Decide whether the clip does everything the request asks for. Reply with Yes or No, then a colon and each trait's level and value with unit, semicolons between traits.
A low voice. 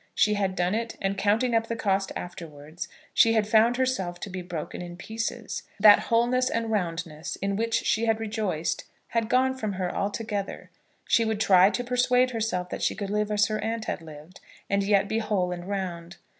No: high, 205 Hz